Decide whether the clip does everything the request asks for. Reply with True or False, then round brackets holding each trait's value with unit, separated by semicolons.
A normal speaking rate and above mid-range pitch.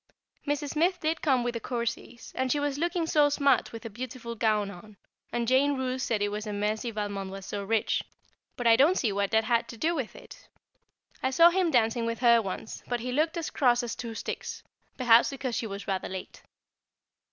False (215 wpm; 240 Hz)